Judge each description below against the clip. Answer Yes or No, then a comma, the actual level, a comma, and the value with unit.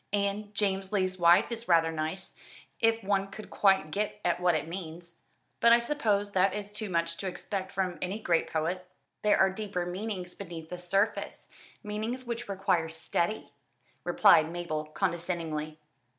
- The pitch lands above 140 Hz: Yes, high, 190 Hz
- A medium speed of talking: Yes, average, 160 wpm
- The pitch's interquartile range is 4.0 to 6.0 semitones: No, average, 3.4 semitones